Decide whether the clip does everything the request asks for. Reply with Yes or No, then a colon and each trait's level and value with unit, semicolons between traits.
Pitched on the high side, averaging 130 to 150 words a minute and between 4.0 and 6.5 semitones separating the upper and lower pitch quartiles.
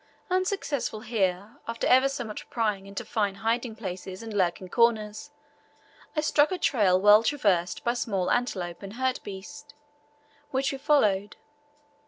Yes: high, 220 Hz; average, 140 wpm; average, 4.9 semitones